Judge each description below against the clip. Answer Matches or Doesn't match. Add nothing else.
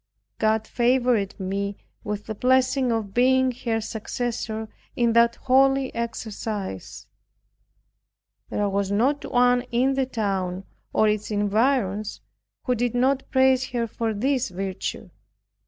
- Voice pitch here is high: Matches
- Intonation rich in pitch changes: Doesn't match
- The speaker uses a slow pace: Matches